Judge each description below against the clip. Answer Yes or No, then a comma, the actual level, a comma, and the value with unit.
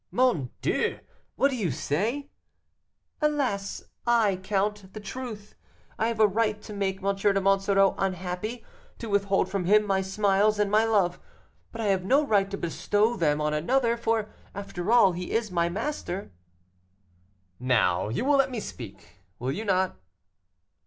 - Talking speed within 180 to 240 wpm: No, average, 160 wpm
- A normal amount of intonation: Yes, average, 3.1 semitones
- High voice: Yes, high, 200 Hz